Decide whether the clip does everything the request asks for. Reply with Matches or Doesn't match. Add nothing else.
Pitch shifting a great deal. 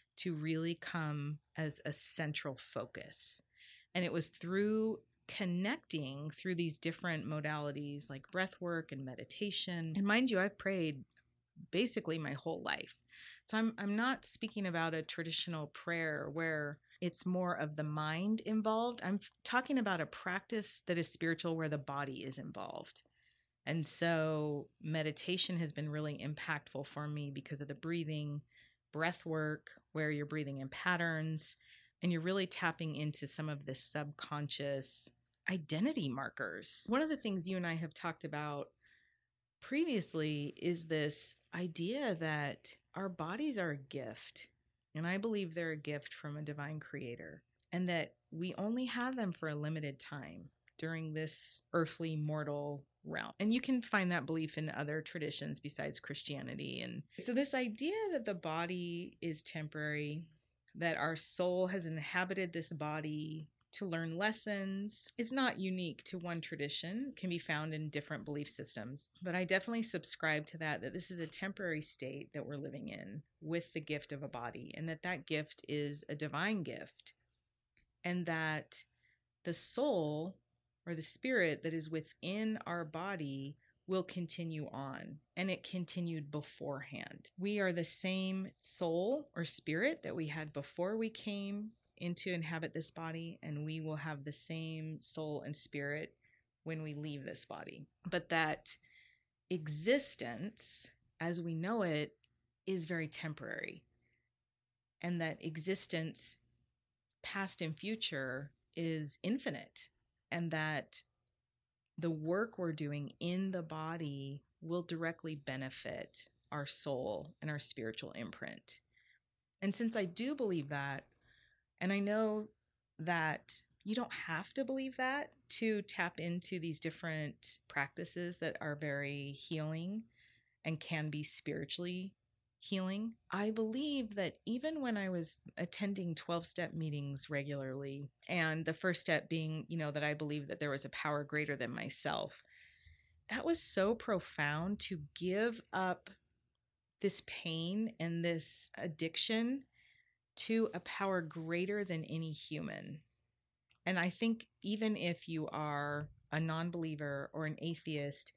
Doesn't match